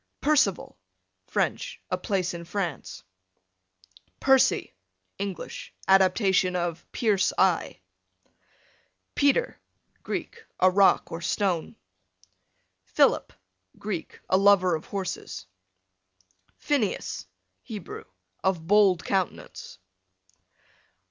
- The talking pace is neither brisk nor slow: No, slow, 80 wpm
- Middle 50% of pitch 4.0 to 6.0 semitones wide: No, average, 2.8 semitones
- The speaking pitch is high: Yes, high, 195 Hz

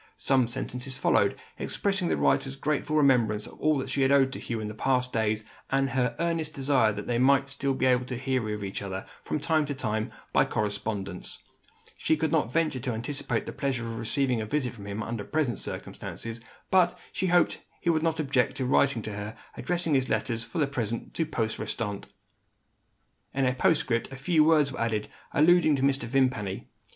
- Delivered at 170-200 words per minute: Yes, average, 195 wpm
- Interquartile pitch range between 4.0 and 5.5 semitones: Yes, average, 4.3 semitones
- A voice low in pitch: Yes, low, 130 Hz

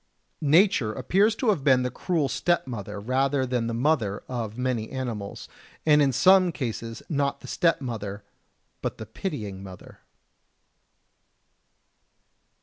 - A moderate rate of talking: No, slow, 125 wpm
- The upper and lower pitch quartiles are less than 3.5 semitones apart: No, wide, 5.4 semitones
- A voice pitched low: Yes, low, 130 Hz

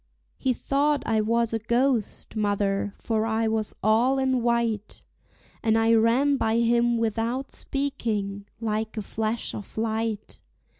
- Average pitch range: No, narrow, 1.7 semitones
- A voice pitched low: No, high, 225 Hz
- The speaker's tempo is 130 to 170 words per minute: Yes, average, 140 wpm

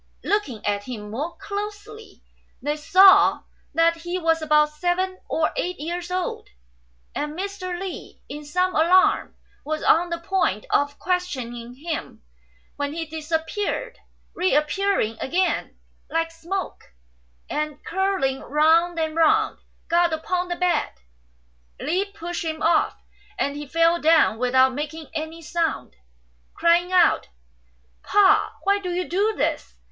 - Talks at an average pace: No, slow, 130 wpm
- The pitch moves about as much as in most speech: Yes, average, 3.4 semitones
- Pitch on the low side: No, very high, 335 Hz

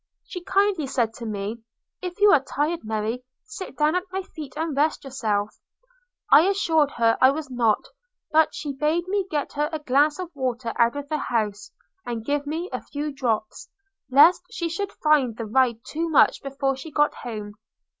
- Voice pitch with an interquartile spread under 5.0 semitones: No, average, 5.3 semitones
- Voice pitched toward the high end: Yes, very high, 285 Hz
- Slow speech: No, average, 190 wpm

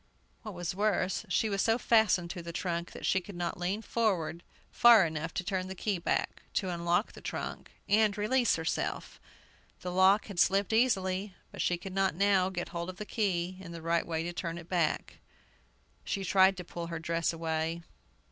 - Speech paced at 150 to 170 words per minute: No, average, 195 wpm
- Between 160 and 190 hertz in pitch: Yes, medium, 185 Hz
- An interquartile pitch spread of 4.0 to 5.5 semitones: No, average, 2.8 semitones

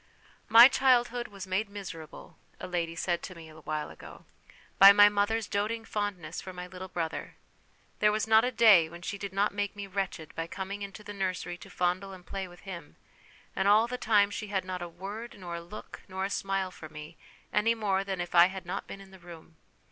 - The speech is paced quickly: Yes, fast, 225 wpm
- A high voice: Yes, high, 195 Hz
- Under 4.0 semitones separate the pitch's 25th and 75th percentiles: Yes, average, 2.7 semitones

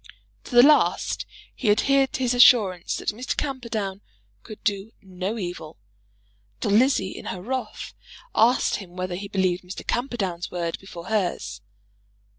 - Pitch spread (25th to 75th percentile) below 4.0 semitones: No, average, 4.9 semitones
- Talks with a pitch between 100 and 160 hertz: No, high, 200 Hz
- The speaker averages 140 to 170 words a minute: Yes, average, 145 wpm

